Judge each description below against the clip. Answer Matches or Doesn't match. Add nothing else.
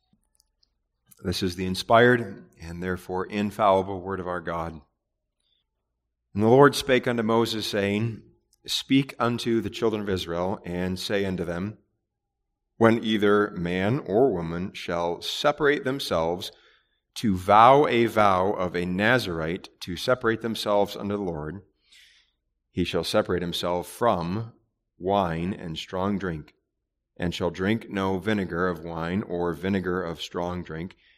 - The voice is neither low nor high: Doesn't match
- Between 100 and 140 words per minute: Matches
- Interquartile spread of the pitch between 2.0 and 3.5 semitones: Doesn't match